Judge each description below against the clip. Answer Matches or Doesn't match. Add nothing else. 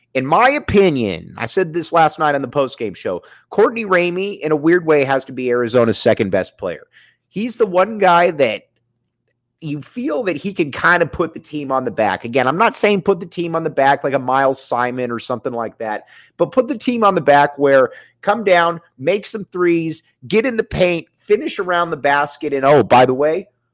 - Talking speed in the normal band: Doesn't match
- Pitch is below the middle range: Doesn't match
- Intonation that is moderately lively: Doesn't match